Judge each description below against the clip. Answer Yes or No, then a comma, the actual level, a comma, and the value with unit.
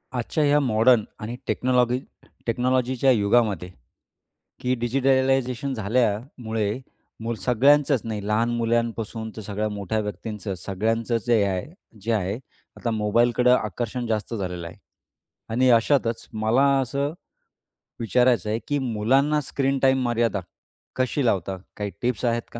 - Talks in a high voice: No, low, 115 Hz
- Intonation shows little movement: No, average, 3.0 semitones